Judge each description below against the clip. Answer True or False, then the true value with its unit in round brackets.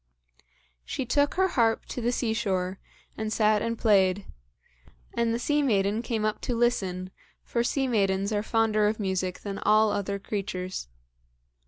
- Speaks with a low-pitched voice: False (215 Hz)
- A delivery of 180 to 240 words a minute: False (160 wpm)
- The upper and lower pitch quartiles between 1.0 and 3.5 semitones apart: True (3.0 semitones)